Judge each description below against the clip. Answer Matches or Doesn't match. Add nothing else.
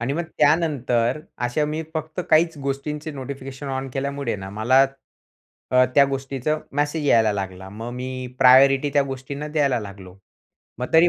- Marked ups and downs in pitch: Doesn't match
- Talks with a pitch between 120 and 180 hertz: Matches